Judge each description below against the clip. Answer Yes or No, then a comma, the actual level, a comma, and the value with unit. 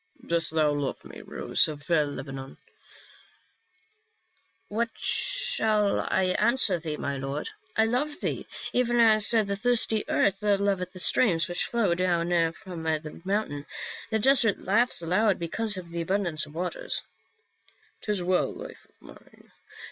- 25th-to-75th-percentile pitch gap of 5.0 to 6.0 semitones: Yes, wide, 5.4 semitones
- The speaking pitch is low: No, high, 195 Hz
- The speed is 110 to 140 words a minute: No, average, 150 wpm